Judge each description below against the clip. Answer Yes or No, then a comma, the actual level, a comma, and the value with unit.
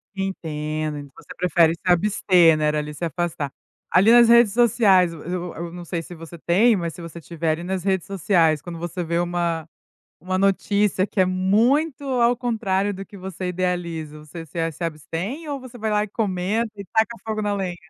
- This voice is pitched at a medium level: Yes, medium, 180 Hz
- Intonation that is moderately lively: Yes, average, 3.7 semitones